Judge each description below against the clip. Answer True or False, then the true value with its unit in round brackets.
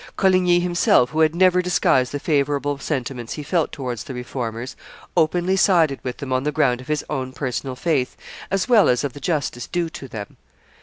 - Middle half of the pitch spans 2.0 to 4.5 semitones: False (5.3 semitones)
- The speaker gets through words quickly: False (195 wpm)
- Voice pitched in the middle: True (145 Hz)